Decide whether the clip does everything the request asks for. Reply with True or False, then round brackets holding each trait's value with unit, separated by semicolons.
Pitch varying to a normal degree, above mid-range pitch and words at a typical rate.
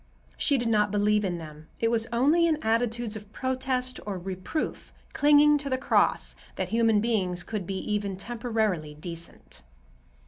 True (4.7 semitones; 220 Hz; 160 wpm)